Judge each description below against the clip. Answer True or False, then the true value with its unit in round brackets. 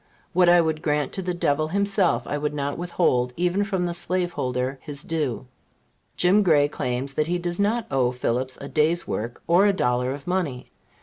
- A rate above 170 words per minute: True (190 wpm)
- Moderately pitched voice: True (155 Hz)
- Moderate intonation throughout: True (4.8 semitones)